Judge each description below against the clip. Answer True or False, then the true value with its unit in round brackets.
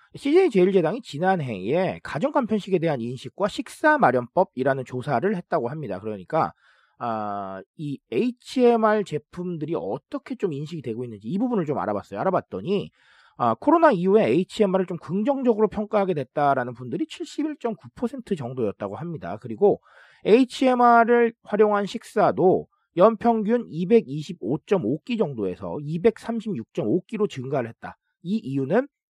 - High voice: True (195 Hz)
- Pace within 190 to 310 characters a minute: True (305 characters per minute)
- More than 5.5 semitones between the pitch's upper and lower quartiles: True (8.6 semitones)